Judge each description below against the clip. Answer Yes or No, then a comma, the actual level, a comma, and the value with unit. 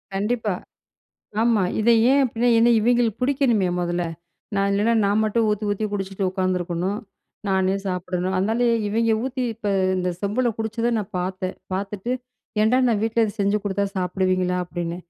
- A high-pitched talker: Yes, high, 205 Hz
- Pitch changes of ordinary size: Yes, average, 3.5 semitones